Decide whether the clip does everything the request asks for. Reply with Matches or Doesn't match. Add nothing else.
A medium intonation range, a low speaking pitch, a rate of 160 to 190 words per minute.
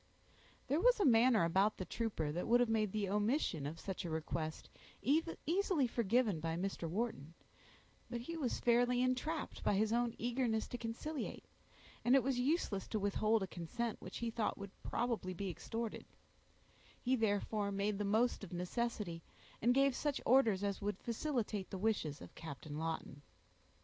Doesn't match